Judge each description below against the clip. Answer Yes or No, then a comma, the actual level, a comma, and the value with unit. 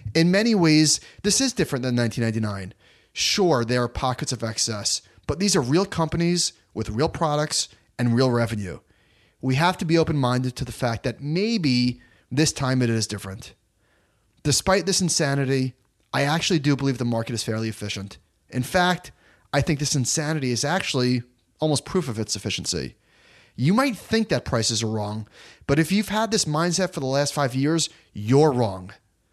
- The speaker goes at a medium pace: Yes, average, 175 wpm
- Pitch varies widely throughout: Yes, wide, 6.3 semitones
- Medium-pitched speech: No, low, 130 Hz